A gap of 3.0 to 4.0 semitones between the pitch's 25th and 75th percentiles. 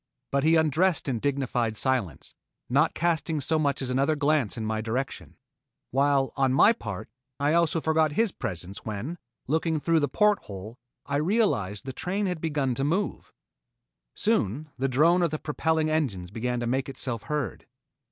No: average, 4.7 semitones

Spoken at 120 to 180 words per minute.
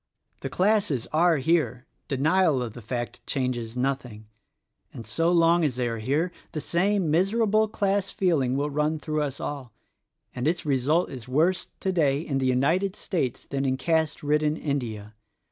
Yes: average, 170 wpm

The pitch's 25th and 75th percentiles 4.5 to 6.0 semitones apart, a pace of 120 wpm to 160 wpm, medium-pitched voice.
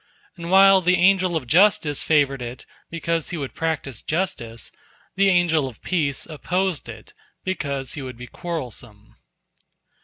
Yes: average, 5.2 semitones; average, 145 wpm; medium, 160 Hz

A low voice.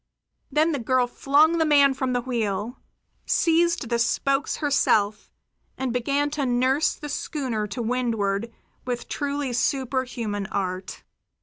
No: very high, 255 Hz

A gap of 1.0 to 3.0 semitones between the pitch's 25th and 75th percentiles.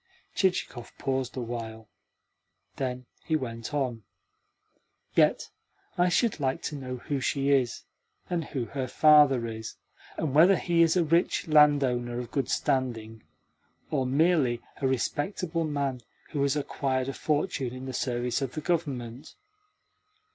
No: average, 3.7 semitones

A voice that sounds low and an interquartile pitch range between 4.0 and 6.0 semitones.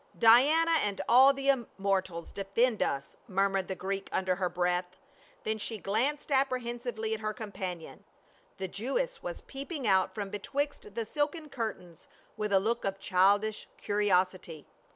No: high, 210 Hz; average, 4.6 semitones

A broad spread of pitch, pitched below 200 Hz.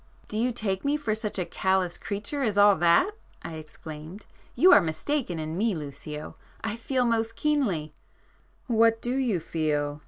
No: wide, 6.6 semitones; high, 205 Hz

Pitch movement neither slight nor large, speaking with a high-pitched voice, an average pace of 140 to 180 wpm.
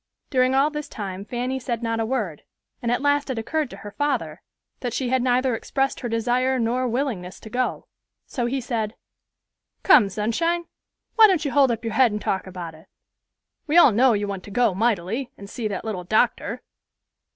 No: average, 3.9 semitones; high, 240 Hz; average, 195 wpm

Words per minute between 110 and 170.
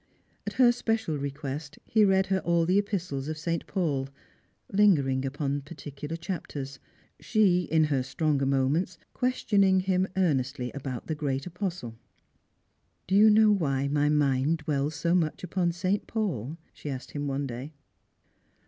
Yes: average, 155 wpm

